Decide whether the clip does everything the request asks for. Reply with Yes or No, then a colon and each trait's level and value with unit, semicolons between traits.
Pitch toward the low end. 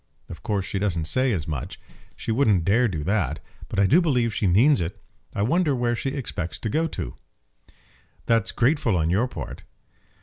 Yes: low, 110 Hz